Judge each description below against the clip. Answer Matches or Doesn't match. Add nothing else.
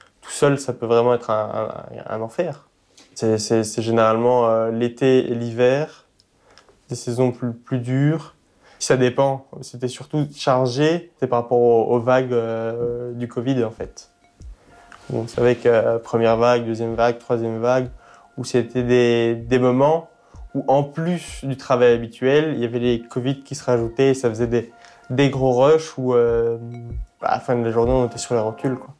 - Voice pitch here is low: Matches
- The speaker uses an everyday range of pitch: Doesn't match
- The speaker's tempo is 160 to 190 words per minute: Matches